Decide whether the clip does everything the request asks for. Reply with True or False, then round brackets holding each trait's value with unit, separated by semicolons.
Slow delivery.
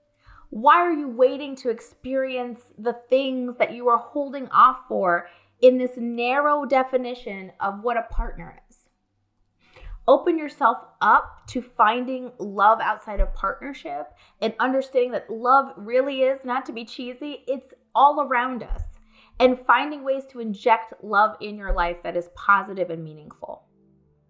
False (150 wpm)